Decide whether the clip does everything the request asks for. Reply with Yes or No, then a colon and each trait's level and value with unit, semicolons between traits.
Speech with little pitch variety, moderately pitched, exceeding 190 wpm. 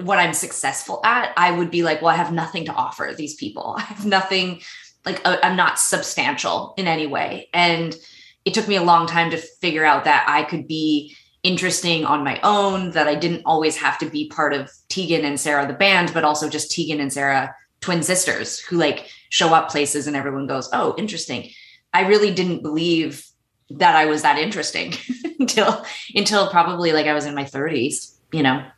No: average, 3.4 semitones; medium, 165 Hz; average, 200 wpm